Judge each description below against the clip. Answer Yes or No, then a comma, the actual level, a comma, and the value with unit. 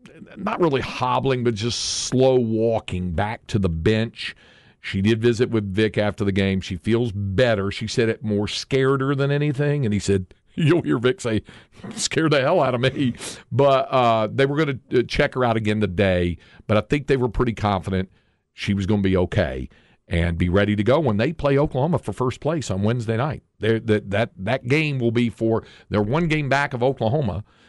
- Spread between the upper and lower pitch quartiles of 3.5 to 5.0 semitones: Yes, average, 4.5 semitones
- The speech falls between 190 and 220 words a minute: Yes, fast, 205 wpm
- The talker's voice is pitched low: Yes, low, 115 Hz